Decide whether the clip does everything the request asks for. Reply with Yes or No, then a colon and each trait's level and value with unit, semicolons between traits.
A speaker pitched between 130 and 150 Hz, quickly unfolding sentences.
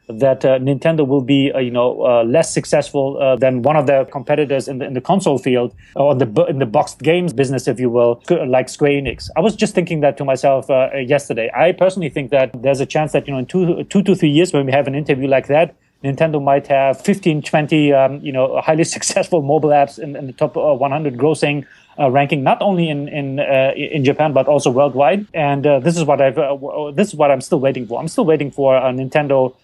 Yes: medium, 140 Hz; fast, 245 wpm